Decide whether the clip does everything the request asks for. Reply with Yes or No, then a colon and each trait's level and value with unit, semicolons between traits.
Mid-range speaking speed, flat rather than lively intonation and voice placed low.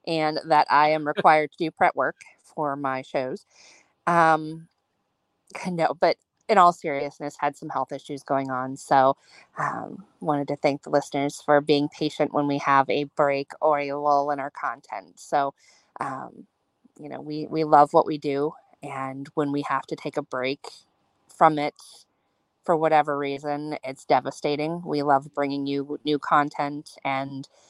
No: average, 165 wpm; narrow, 1.5 semitones; medium, 145 Hz